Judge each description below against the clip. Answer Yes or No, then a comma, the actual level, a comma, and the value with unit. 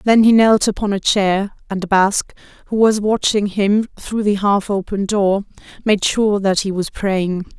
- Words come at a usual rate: Yes, average, 180 wpm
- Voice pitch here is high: Yes, high, 200 Hz